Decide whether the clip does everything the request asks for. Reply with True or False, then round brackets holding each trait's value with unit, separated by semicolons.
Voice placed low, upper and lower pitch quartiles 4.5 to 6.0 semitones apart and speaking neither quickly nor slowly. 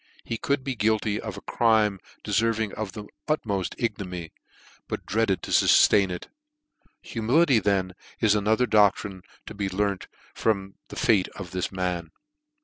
False (105 Hz; 2.8 semitones; 145 wpm)